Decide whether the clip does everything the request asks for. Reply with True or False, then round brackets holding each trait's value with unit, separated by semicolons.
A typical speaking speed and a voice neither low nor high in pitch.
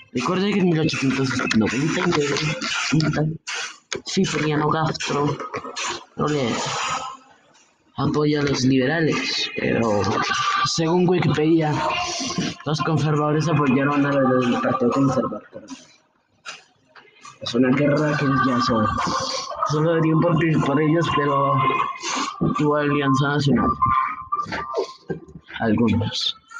False (85 wpm; 150 Hz)